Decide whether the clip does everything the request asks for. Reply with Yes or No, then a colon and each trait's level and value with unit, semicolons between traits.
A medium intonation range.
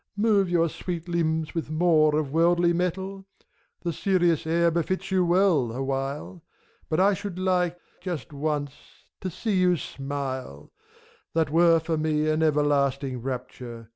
Yes: average, 3.8 semitones